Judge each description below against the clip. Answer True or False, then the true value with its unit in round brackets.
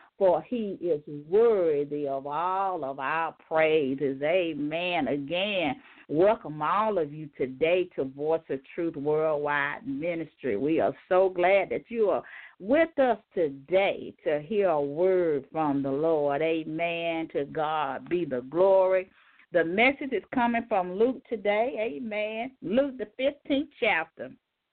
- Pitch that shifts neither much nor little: False (6.4 semitones)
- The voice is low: False (175 Hz)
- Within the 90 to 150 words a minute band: True (140 wpm)